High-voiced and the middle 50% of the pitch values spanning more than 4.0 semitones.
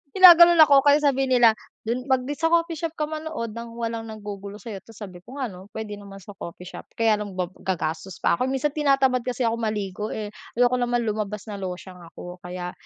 Yes: high, 230 Hz; average, 5.2 semitones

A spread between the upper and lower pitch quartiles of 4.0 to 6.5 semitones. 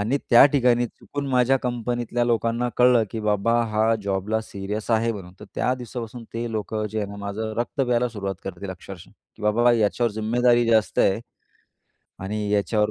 No: narrow, 2.6 semitones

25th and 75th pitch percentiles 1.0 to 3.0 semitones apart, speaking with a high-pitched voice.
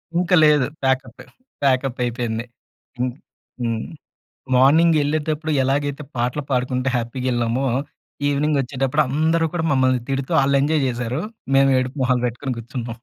No: average, 2.7 semitones; low, 130 Hz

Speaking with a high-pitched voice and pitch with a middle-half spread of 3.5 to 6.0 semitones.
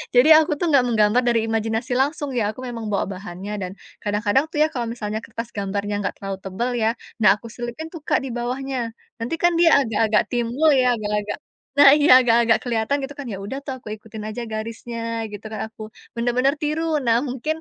Yes: high, 235 Hz; average, 3.8 semitones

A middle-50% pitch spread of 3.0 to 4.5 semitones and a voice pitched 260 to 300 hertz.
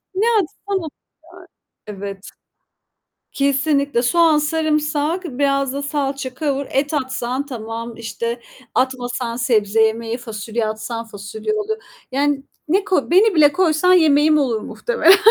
No: average, 5.0 semitones; very high, 275 Hz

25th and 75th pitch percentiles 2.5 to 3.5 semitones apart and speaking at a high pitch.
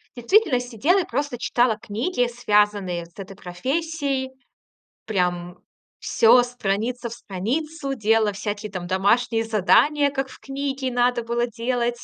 No: average, 4.3 semitones; high, 240 Hz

